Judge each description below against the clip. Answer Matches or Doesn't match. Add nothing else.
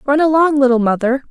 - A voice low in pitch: Doesn't match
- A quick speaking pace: Doesn't match